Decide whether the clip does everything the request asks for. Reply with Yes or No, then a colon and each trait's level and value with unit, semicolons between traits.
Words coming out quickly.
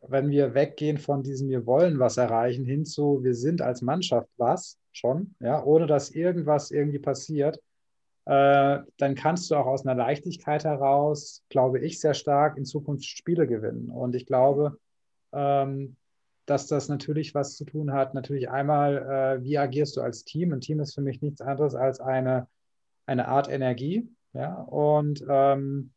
No: average, 170 wpm